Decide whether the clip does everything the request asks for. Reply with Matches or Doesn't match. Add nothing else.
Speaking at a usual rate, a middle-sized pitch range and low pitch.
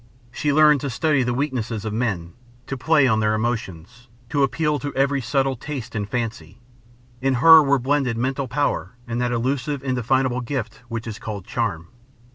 Matches